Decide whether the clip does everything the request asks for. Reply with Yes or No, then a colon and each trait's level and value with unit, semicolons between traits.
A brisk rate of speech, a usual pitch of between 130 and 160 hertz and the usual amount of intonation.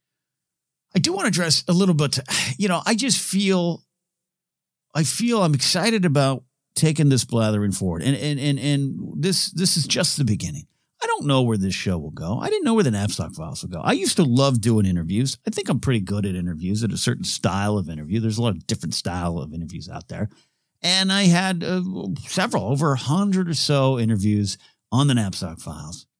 No: fast, 215 wpm; medium, 140 Hz; wide, 8.7 semitones